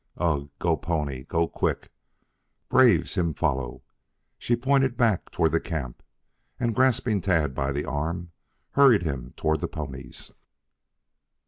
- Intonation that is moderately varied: No, wide, 6.8 semitones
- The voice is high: No, very low, 85 Hz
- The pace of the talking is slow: Yes, slow, 130 wpm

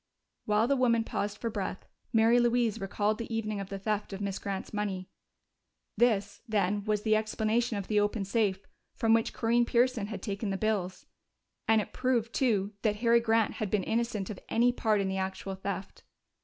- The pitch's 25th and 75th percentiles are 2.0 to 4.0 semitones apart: Yes, narrow, 2.5 semitones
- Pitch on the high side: Yes, high, 215 Hz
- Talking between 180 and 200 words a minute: Yes, average, 190 wpm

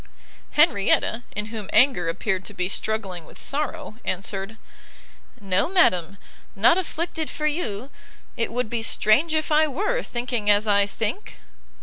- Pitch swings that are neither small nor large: No, wide, 7.3 semitones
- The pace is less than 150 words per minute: Yes, average, 140 wpm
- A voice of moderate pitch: No, high, 225 Hz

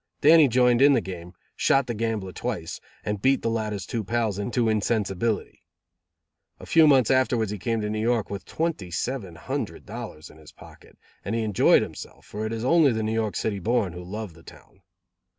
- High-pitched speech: No, low, 110 Hz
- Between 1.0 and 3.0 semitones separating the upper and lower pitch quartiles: No, average, 3.6 semitones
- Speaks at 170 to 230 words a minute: Yes, average, 200 wpm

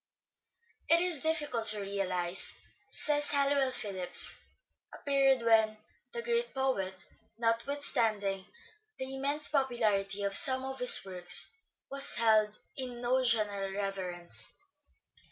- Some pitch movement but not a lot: No, wide, 5.8 semitones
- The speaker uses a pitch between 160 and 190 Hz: No, high, 235 Hz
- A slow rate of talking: Yes, slow, 120 wpm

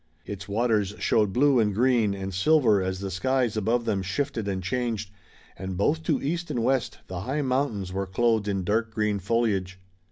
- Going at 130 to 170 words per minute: No, average, 185 wpm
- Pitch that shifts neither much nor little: Yes, average, 4.2 semitones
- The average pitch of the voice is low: Yes, low, 105 Hz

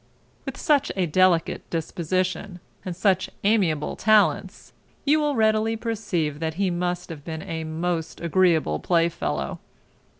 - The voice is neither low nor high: Yes, medium, 180 Hz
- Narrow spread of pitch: No, average, 3.8 semitones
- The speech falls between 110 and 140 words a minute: Yes, slow, 135 wpm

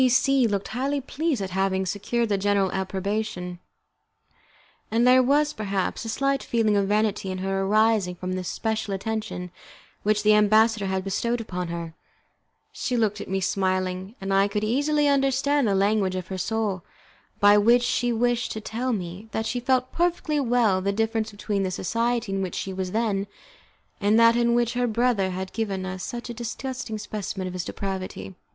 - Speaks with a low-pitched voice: No, high, 215 Hz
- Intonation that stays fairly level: No, average, 3.8 semitones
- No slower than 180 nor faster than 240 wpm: Yes, average, 185 wpm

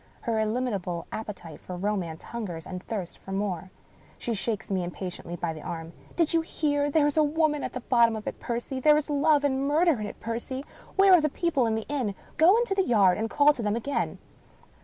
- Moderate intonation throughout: No, wide, 7.1 semitones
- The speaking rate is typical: No, fast, 220 wpm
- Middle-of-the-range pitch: No, high, 235 Hz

